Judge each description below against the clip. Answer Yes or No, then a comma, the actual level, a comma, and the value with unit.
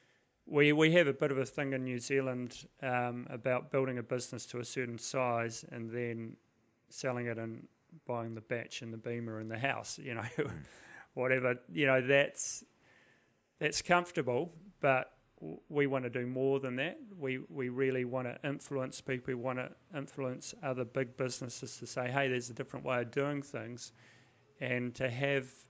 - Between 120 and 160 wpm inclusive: No, average, 180 wpm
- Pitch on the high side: No, low, 130 Hz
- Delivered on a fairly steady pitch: Yes, narrow, 2.1 semitones